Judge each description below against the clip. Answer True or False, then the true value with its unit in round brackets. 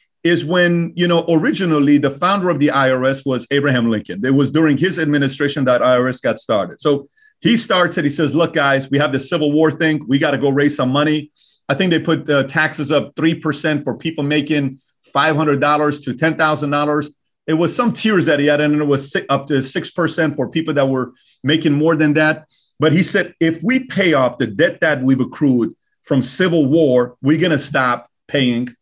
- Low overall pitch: False (150 Hz)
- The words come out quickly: True (215 wpm)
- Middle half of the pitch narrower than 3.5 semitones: True (2.8 semitones)